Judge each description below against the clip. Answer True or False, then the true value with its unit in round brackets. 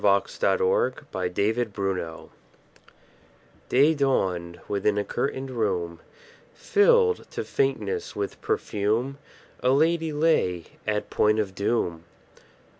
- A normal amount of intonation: False (7.4 semitones)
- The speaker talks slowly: True (120 wpm)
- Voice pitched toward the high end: False (110 Hz)